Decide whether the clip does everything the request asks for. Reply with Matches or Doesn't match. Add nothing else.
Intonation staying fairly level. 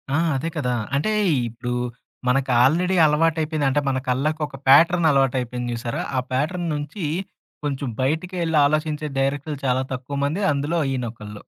Doesn't match